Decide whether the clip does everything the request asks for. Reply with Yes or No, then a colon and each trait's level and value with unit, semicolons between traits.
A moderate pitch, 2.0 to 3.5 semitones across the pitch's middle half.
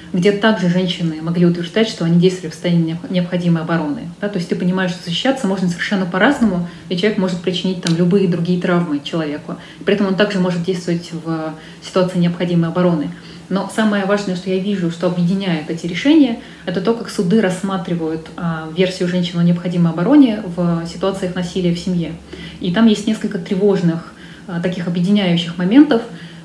Yes: medium, 180 Hz; narrow, 2.4 semitones